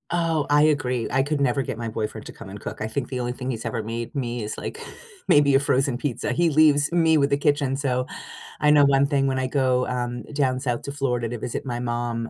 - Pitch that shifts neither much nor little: Yes, average, 3.0 semitones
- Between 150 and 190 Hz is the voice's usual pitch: No, low, 130 Hz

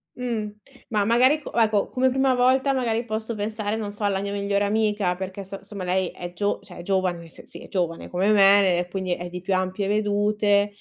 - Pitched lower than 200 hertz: No, high, 205 Hz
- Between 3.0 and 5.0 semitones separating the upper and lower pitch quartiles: No, narrow, 2.6 semitones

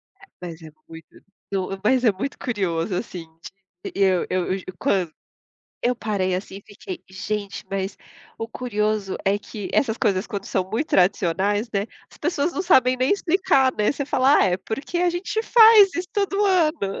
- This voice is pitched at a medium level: No, high, 215 Hz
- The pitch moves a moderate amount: No, wide, 7.7 semitones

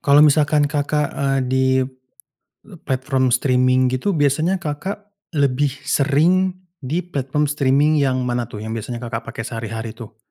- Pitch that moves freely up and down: No, average, 2.9 semitones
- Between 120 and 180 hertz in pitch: Yes, low, 135 Hz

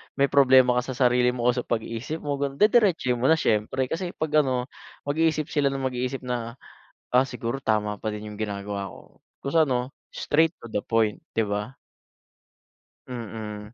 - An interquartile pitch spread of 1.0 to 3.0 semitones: No, average, 3.9 semitones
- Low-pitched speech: Yes, low, 125 Hz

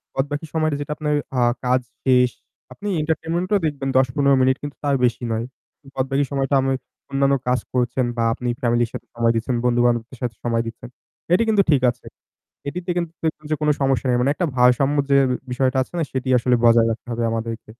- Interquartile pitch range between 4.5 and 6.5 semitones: No, average, 3.0 semitones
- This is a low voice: Yes, low, 130 Hz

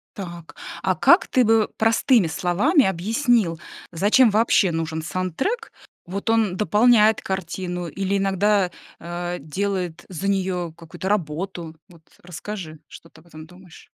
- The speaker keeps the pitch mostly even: No, average, 3.6 semitones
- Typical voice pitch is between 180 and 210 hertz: Yes, medium, 185 Hz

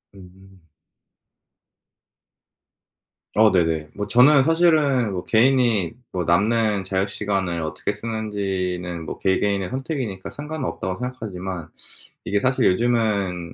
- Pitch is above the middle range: No, low, 100 Hz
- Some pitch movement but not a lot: Yes, average, 4.8 semitones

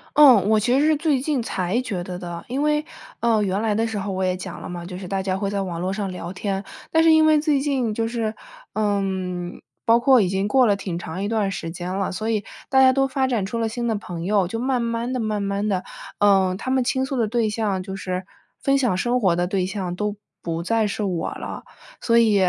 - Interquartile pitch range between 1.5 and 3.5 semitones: No, average, 4.4 semitones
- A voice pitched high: Yes, high, 210 Hz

